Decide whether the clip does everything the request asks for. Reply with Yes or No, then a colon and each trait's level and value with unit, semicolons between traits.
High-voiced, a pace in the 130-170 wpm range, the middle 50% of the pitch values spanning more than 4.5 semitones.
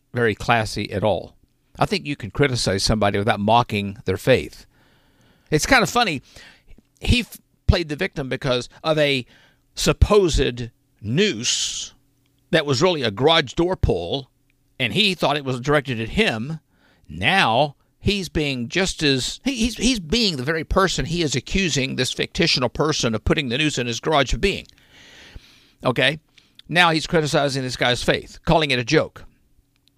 No: medium, 140 Hz; average, 160 wpm; average, 5.2 semitones